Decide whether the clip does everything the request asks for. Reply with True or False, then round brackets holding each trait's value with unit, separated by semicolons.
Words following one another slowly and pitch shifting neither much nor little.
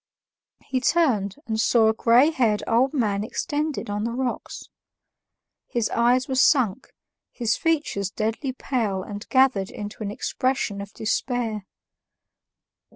True (130 wpm; 3.9 semitones)